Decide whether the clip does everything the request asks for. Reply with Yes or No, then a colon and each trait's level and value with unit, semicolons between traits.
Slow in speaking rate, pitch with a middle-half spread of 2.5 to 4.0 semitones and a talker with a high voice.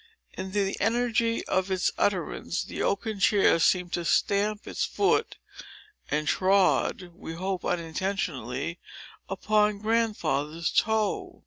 Yes: slow, 115 wpm; average, 3.6 semitones; high, 195 Hz